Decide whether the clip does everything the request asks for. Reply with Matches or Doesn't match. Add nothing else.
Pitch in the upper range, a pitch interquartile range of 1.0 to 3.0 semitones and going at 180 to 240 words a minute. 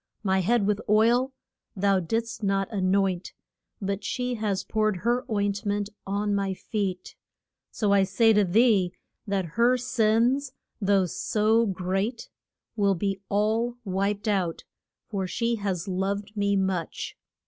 Doesn't match